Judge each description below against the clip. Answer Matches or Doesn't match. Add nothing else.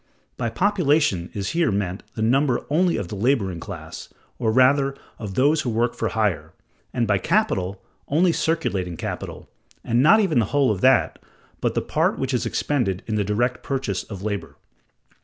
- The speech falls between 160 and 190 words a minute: Matches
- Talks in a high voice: Doesn't match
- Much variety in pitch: Matches